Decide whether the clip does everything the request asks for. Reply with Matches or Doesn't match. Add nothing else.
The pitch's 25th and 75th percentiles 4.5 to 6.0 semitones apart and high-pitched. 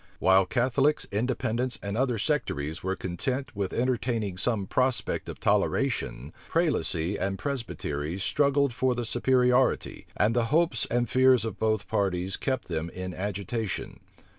Doesn't match